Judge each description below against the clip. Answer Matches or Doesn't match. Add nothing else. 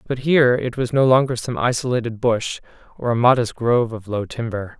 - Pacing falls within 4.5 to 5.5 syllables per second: Doesn't match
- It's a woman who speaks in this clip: Doesn't match